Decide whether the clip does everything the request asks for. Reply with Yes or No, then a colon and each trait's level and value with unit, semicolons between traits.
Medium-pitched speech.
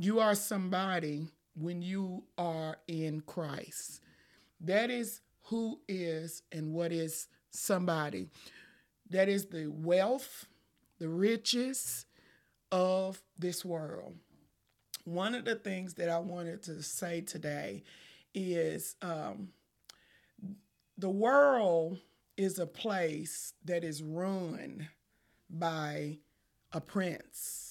Yes: medium, 175 Hz